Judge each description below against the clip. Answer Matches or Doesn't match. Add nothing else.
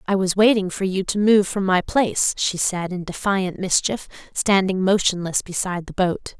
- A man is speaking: Doesn't match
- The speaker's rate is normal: Matches